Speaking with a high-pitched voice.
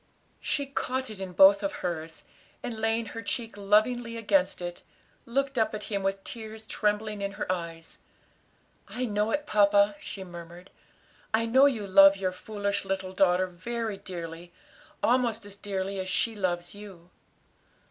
Yes: high, 200 Hz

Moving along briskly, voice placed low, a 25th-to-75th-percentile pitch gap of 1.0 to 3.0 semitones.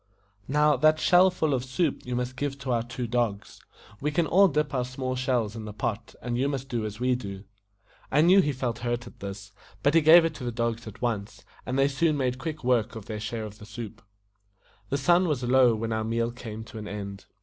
No: fast, 240 wpm; low, 125 Hz; average, 4.1 semitones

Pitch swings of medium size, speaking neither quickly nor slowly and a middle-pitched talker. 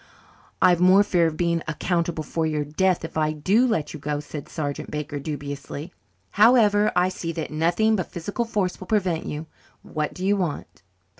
Yes: average, 3.8 semitones; average, 180 wpm; medium, 170 Hz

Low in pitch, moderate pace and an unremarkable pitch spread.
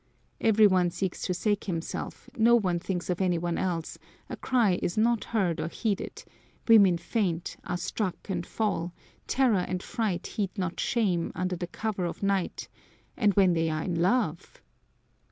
No: medium, 185 Hz; average, 170 wpm; average, 3.5 semitones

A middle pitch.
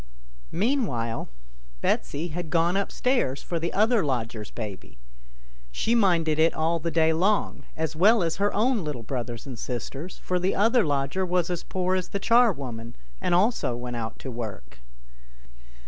Yes: medium, 165 Hz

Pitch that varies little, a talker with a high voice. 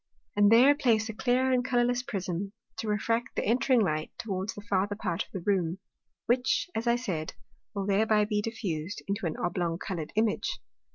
No: average, 4.0 semitones; high, 210 Hz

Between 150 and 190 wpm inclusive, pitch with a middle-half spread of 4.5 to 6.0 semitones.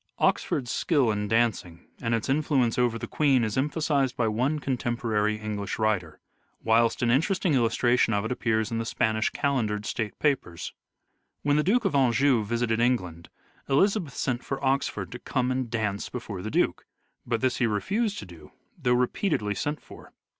No: average, 170 wpm; average, 4.0 semitones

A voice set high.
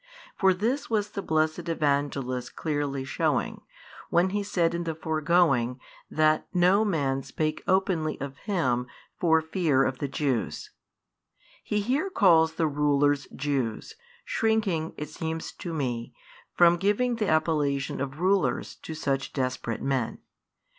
No: medium, 160 Hz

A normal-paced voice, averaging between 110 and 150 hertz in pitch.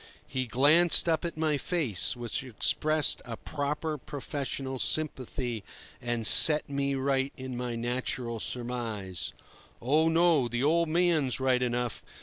No: slow, 130 wpm; low, 135 Hz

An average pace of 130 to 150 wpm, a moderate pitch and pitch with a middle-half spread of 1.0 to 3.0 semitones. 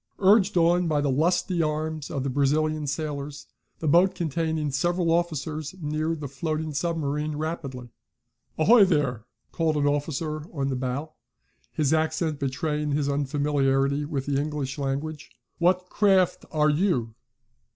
Yes: average, 140 wpm; medium, 150 Hz; narrow, 2.6 semitones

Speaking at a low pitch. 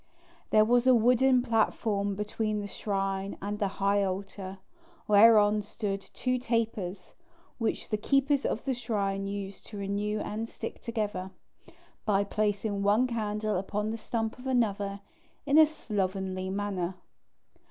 No: high, 210 Hz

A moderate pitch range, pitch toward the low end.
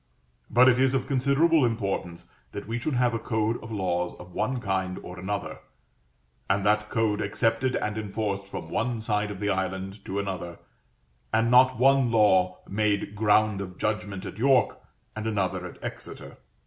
Yes: average, 3.5 semitones; low, 105 Hz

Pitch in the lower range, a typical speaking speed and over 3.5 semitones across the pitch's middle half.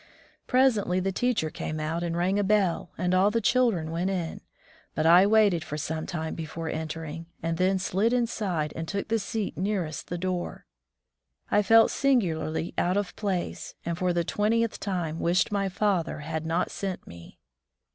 No: medium, 180 Hz; average, 175 wpm; average, 3.9 semitones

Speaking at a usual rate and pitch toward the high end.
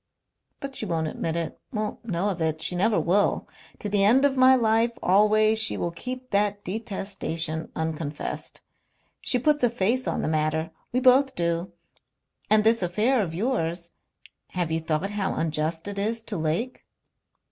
Yes: average, 170 wpm; high, 200 Hz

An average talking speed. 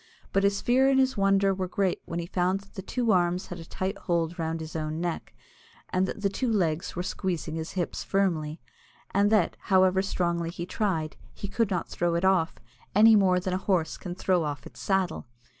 No: fast, 210 wpm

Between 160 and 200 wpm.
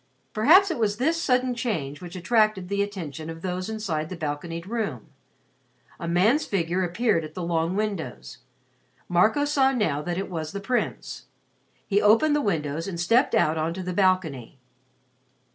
Yes: average, 165 wpm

